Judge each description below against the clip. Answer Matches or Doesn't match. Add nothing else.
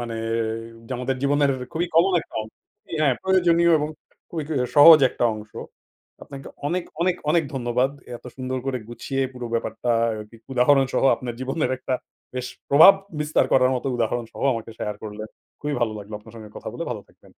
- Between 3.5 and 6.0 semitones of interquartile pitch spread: Matches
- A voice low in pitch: Matches